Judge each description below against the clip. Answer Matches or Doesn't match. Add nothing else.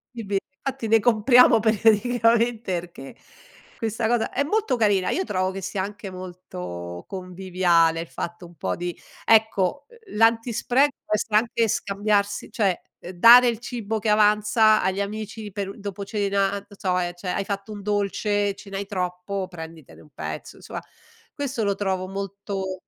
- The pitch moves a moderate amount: Matches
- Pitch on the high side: Matches